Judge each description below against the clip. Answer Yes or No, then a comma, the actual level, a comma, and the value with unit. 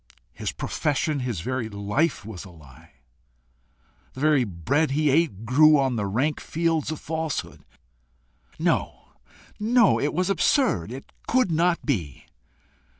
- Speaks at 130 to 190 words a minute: Yes, slow, 135 wpm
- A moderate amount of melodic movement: No, wide, 7.6 semitones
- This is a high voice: No, medium, 140 Hz